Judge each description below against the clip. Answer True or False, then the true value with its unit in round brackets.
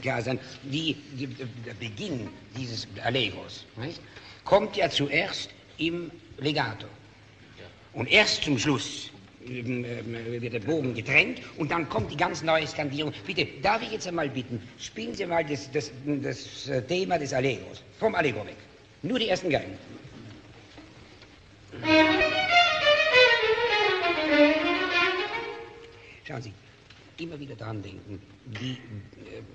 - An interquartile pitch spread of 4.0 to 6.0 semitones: False (7.2 semitones)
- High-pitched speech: False (135 Hz)